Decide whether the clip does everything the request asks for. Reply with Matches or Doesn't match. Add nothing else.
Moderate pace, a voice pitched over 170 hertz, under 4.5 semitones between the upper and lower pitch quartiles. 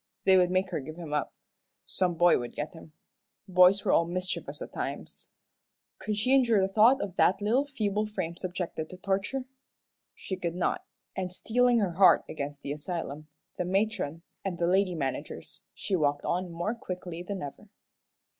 Matches